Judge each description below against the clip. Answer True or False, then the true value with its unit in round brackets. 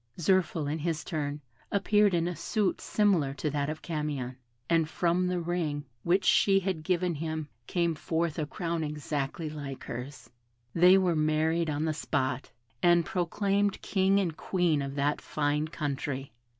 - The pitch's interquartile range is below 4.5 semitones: True (3.3 semitones)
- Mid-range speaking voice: True (160 Hz)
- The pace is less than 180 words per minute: True (160 wpm)